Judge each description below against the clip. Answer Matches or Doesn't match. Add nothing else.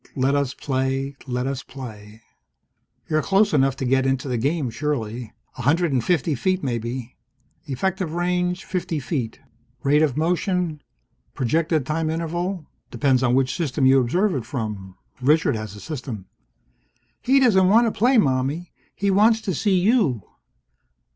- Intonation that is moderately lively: Doesn't match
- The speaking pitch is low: Doesn't match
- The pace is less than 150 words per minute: Doesn't match